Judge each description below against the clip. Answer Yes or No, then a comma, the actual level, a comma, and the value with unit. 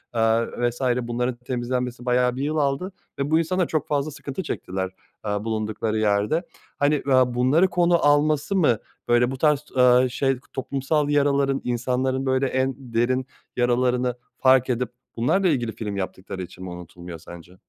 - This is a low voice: Yes, low, 125 Hz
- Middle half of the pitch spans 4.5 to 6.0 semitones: No, average, 3.3 semitones